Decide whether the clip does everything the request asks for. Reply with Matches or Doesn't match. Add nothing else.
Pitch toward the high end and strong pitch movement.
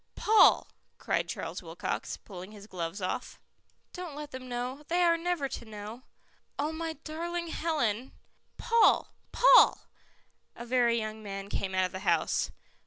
Matches